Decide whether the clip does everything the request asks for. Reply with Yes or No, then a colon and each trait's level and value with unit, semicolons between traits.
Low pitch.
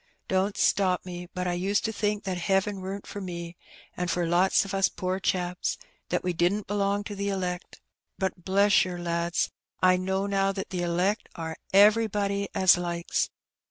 No: high, 190 Hz